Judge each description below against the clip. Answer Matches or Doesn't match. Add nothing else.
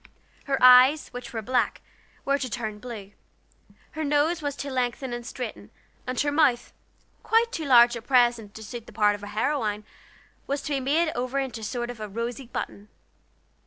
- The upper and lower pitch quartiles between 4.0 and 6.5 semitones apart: Doesn't match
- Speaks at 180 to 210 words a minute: Matches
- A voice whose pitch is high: Matches